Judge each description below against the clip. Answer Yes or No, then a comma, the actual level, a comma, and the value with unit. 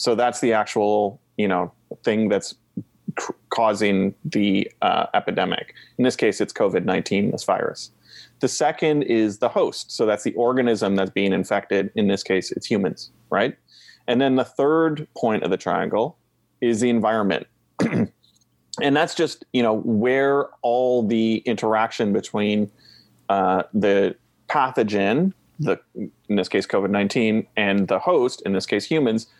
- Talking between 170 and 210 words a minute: No, average, 150 wpm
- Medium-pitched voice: No, low, 110 Hz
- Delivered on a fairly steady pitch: No, average, 3.4 semitones